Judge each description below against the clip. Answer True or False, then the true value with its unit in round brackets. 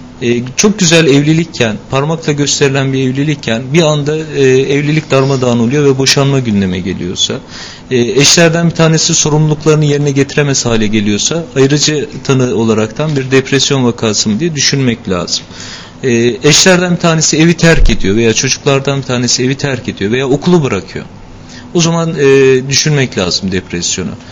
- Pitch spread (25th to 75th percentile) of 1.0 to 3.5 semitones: False (4.1 semitones)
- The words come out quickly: True (150 wpm)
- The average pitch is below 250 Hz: True (135 Hz)